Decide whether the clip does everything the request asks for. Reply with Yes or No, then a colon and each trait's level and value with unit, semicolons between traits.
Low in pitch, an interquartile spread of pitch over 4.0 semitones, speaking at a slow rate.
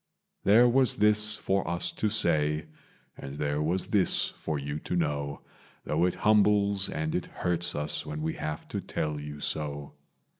No: very low, 80 Hz; average, 5.2 semitones; average, 165 wpm